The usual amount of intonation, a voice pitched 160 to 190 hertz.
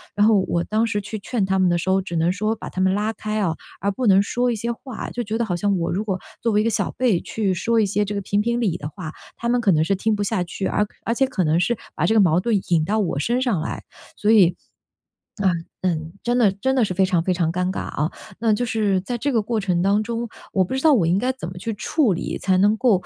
No: average, 3.7 semitones; high, 205 Hz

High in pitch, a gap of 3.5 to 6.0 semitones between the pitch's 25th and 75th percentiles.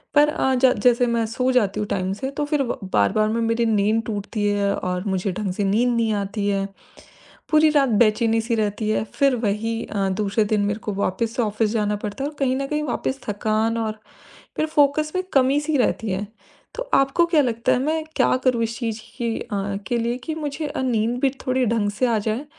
Yes: high, 230 Hz; average, 4.0 semitones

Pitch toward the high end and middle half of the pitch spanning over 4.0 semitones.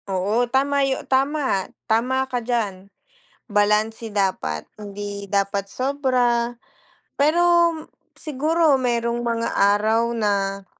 Yes: high, 230 Hz; average, 4.5 semitones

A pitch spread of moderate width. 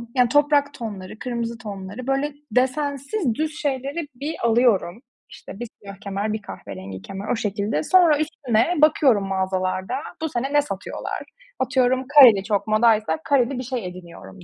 No: wide, 5.9 semitones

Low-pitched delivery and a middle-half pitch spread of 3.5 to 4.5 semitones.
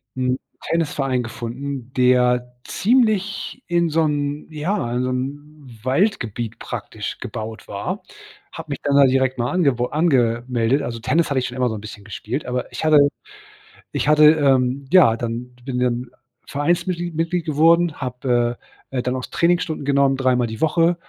Yes: low, 130 Hz; average, 4.0 semitones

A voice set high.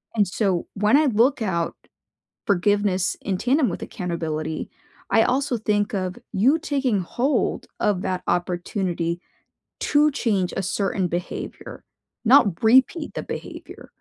Yes: high, 205 Hz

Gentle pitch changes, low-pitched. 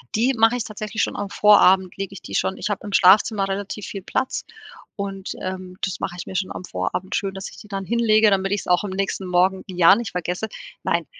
No: narrow, 2.1 semitones; high, 195 Hz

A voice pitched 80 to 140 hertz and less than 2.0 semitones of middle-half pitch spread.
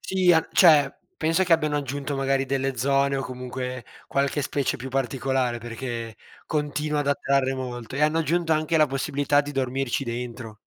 No: low, 135 Hz; narrow, 2.6 semitones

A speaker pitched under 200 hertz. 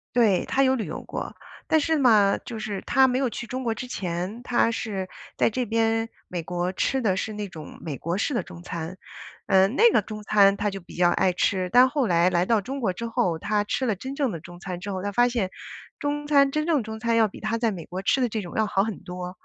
No: high, 215 Hz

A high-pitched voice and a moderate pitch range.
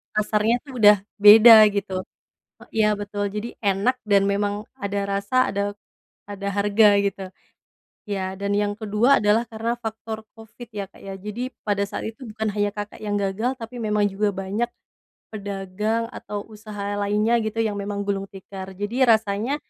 No: high, 210 Hz; narrow, 1.6 semitones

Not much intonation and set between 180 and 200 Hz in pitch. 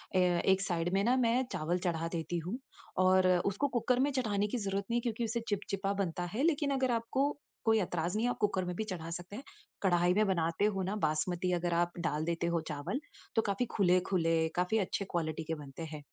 No: average, 4.4 semitones; medium, 185 Hz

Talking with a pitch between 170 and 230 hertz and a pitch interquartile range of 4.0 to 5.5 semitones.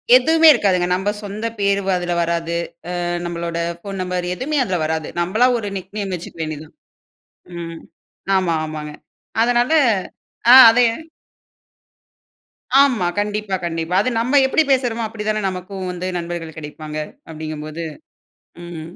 Yes: medium, 185 Hz; average, 4.3 semitones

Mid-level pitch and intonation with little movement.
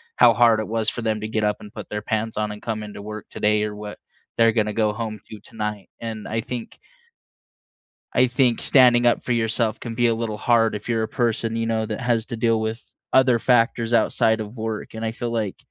No: low, 110 Hz; narrow, 1.6 semitones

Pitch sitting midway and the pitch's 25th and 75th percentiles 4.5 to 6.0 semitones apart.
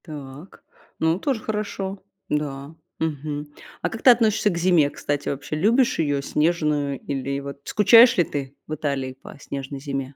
Yes: medium, 150 Hz; average, 5.2 semitones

